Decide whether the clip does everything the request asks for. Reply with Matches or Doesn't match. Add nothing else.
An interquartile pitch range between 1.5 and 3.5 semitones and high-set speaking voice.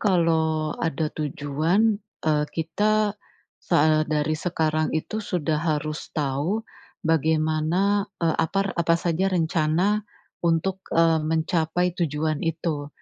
Doesn't match